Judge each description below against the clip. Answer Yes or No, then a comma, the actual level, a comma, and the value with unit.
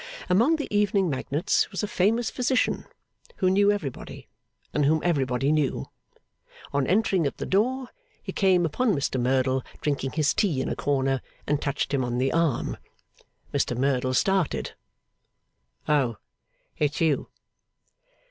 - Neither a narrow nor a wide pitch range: No, wide, 6.5 semitones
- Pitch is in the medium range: Yes, medium, 150 Hz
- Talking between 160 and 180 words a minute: No, average, 140 wpm